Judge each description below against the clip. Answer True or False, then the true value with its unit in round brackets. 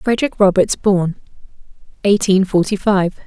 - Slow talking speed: True (110 wpm)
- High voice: True (195 Hz)